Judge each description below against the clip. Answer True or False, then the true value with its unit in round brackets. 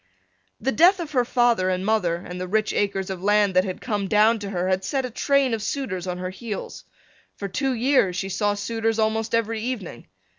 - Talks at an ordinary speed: False (215 wpm)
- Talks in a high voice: True (210 Hz)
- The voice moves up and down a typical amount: True (4.1 semitones)